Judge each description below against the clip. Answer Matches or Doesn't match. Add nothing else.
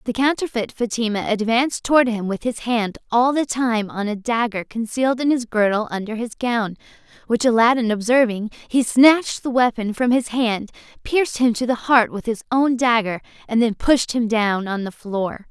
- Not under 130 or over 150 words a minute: Doesn't match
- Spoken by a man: Doesn't match